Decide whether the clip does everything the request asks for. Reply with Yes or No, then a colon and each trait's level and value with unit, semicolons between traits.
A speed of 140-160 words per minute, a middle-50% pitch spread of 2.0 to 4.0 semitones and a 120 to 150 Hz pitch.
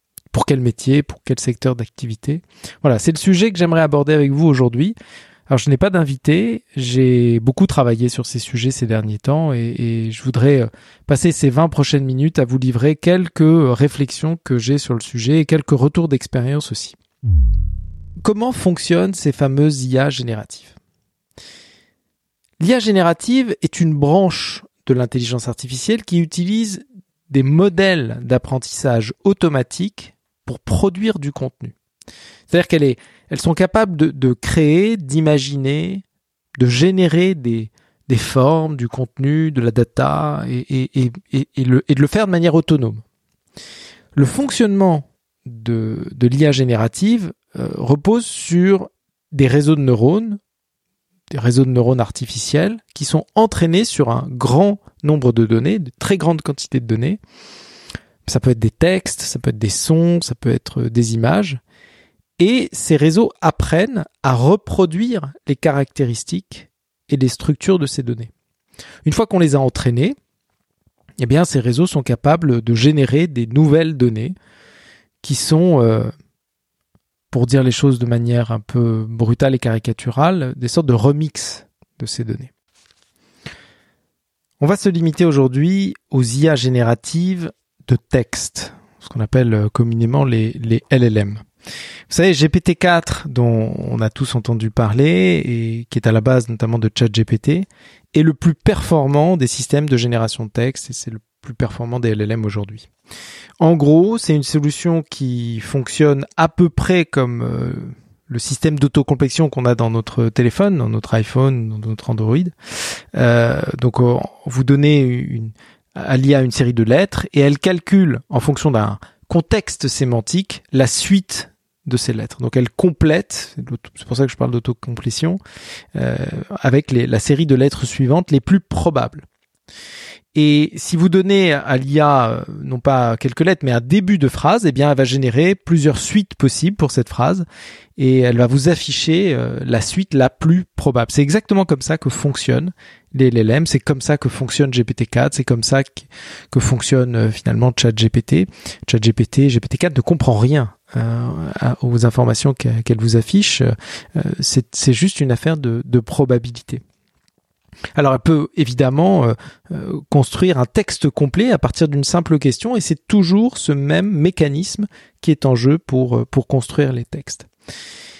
No: average, 155 wpm; average, 5.2 semitones; medium, 140 Hz